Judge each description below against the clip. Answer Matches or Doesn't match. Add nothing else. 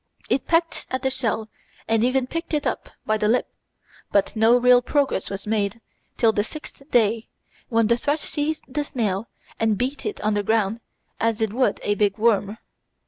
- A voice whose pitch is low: Doesn't match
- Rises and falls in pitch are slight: Doesn't match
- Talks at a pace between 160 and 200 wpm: Matches